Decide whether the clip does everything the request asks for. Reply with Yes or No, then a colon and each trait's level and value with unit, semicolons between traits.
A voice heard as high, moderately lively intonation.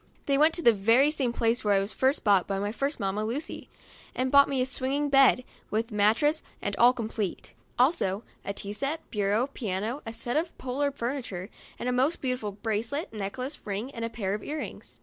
Yes: high, 240 Hz; average, 4.9 semitones